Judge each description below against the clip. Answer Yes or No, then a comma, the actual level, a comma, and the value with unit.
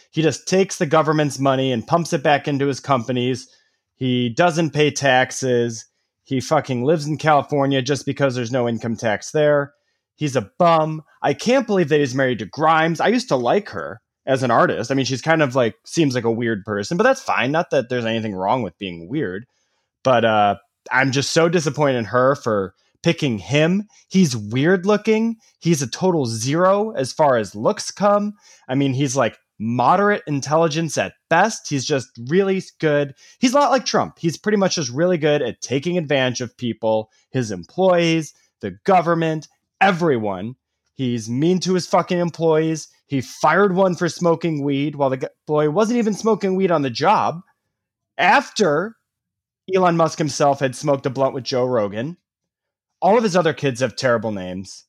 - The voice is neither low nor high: Yes, medium, 145 Hz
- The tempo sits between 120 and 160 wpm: No, average, 185 wpm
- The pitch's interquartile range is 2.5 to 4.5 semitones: No, average, 5.1 semitones